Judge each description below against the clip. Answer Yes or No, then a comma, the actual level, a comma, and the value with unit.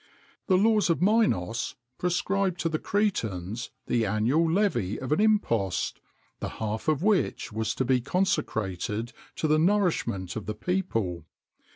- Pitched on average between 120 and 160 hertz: Yes, medium, 140 Hz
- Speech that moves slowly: No, average, 145 wpm